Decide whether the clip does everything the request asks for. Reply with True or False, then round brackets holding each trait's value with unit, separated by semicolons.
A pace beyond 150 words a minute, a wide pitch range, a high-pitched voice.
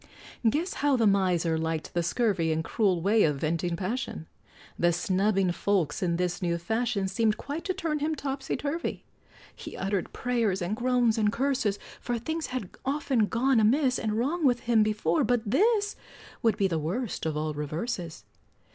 True (175 wpm; 6.4 semitones; 215 Hz)